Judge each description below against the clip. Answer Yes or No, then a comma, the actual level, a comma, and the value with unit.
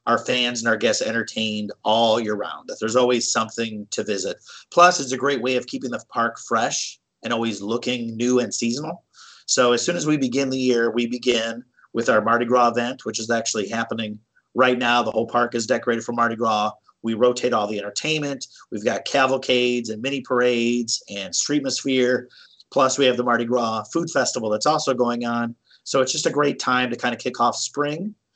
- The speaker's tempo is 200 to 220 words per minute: Yes, fast, 205 wpm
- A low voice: Yes, low, 120 Hz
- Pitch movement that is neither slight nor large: No, narrow, 1.8 semitones